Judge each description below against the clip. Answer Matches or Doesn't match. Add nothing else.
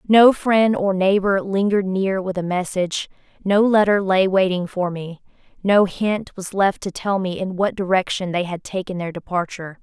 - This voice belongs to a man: Doesn't match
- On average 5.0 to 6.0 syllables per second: Doesn't match